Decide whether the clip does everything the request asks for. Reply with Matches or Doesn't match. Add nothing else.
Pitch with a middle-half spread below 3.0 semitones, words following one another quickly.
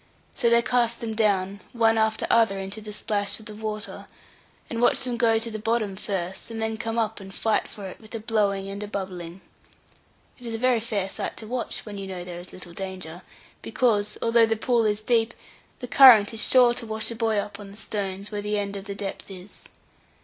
Matches